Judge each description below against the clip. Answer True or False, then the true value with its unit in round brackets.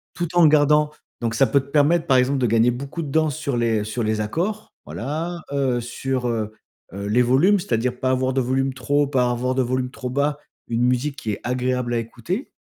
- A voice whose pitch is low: True (130 Hz)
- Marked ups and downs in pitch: False (3.2 semitones)